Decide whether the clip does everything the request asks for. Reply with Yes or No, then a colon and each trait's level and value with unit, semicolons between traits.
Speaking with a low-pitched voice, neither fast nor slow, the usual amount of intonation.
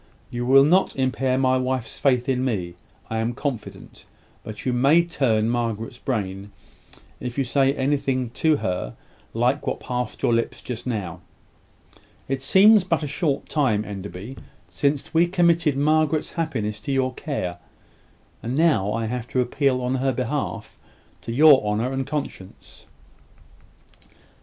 Yes: low, 130 Hz; average, 145 wpm; average, 3.9 semitones